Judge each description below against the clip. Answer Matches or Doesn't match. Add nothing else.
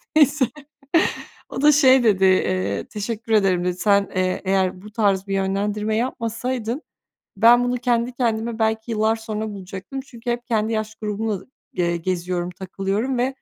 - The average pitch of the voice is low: Doesn't match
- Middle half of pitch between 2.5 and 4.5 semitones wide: Matches